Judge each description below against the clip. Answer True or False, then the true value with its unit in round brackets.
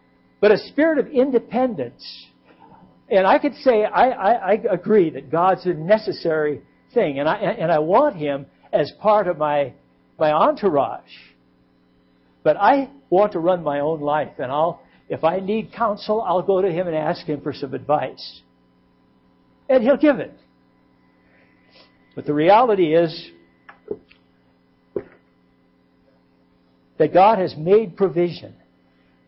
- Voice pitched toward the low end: False (155 Hz)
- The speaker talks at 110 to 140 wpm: True (135 wpm)